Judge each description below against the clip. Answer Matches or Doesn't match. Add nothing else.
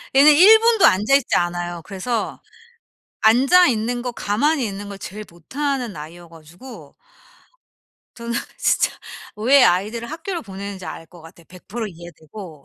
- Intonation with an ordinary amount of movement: Doesn't match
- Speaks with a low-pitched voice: Doesn't match